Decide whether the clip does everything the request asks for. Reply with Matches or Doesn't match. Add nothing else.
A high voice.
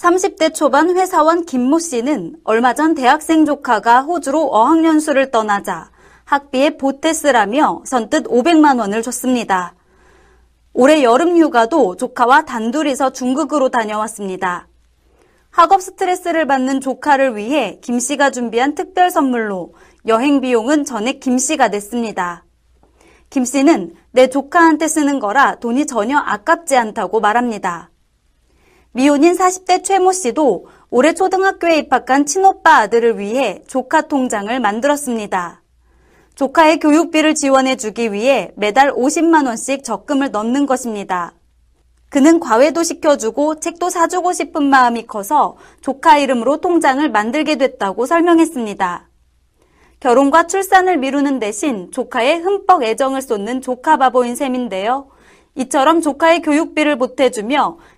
Matches